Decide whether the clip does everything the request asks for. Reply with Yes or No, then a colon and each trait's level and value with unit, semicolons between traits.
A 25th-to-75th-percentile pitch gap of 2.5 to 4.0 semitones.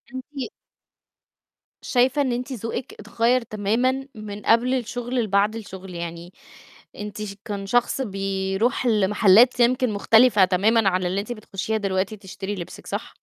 Yes: average, 3.7 semitones